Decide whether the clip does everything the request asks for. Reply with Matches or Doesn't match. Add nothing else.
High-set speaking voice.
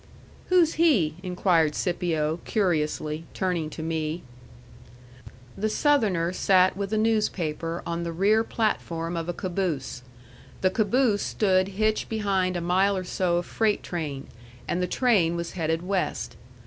Doesn't match